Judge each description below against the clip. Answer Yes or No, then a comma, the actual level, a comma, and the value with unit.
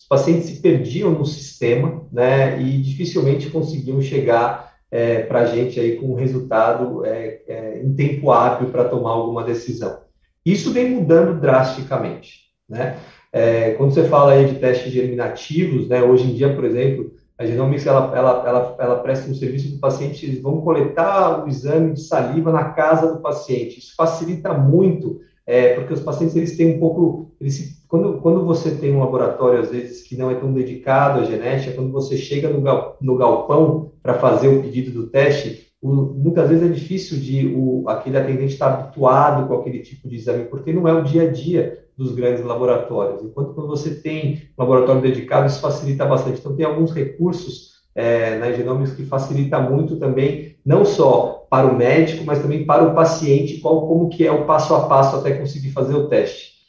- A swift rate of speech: Yes, fast, 195 wpm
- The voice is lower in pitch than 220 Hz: Yes, medium, 140 Hz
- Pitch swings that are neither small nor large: Yes, average, 3.7 semitones